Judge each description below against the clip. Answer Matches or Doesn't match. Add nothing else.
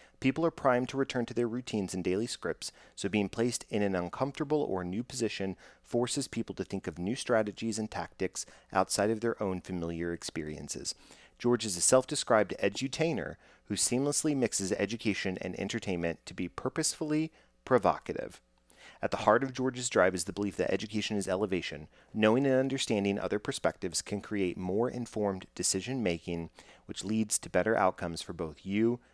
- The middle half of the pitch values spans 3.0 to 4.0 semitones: Doesn't match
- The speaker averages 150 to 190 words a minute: Matches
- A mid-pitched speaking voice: Doesn't match